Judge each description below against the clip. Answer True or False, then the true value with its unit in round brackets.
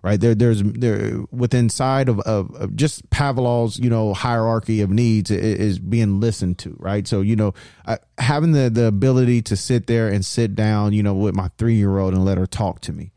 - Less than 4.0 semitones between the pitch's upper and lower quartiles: True (2.9 semitones)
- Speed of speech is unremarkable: False (225 wpm)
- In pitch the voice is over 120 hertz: False (110 Hz)